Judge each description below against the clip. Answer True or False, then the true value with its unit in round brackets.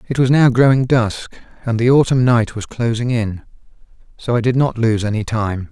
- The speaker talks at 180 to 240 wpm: True (200 wpm)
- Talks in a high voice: False (120 Hz)